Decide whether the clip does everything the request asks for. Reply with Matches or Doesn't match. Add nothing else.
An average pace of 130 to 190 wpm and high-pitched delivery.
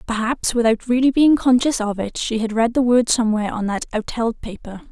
Doesn't match